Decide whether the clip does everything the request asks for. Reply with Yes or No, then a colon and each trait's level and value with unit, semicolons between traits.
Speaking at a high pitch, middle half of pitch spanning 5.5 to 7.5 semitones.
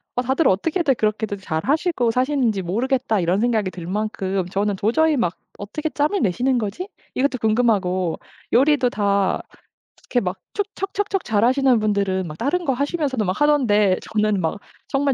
Yes: high, 225 Hz; wide, 5.8 semitones